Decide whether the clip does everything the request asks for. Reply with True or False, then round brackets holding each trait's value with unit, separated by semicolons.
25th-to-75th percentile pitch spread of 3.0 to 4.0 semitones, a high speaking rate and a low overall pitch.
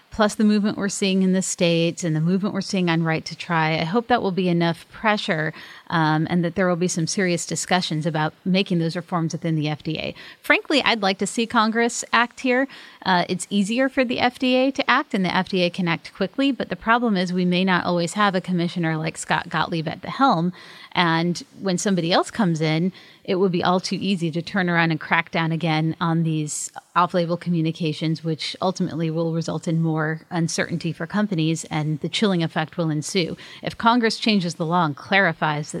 False (3.3 semitones; 210 wpm; 175 Hz)